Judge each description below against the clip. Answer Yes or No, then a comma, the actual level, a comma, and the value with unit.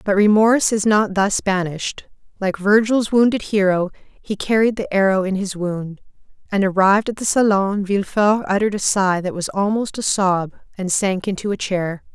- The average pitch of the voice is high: Yes, high, 200 Hz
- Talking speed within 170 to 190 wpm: Yes, average, 180 wpm